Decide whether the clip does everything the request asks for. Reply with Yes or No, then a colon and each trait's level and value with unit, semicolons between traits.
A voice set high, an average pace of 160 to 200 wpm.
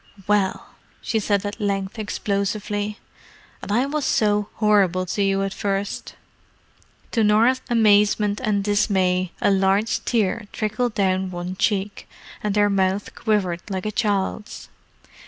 No: high, 205 Hz; slow, 135 wpm